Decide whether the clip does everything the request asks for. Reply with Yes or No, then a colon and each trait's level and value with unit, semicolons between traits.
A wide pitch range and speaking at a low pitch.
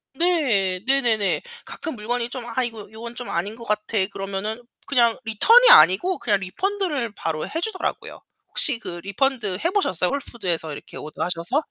No: wide, 5.9 semitones; high, 230 Hz